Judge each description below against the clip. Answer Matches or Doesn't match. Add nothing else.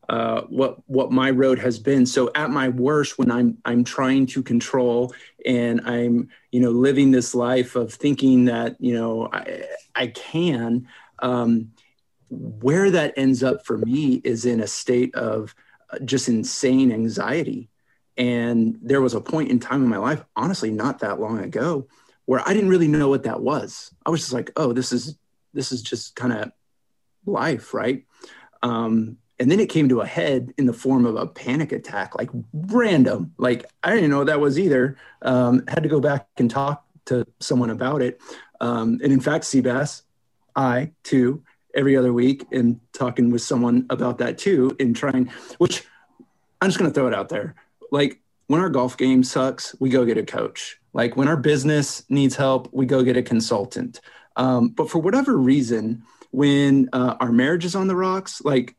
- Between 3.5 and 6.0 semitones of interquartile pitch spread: Doesn't match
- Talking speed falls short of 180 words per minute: Doesn't match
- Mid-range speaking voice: Doesn't match